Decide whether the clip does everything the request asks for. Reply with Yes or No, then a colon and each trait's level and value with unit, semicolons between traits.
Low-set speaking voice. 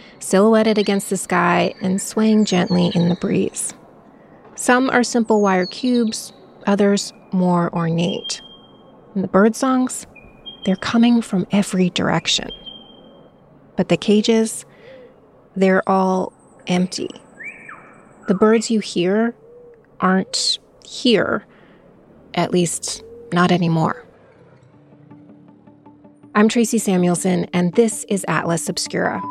No: high, 200 Hz